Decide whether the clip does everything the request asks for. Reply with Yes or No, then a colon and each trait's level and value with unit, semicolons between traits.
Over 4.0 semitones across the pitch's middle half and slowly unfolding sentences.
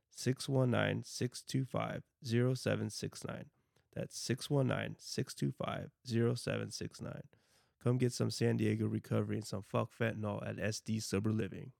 No: average, 2.7 semitones; slow, 85 wpm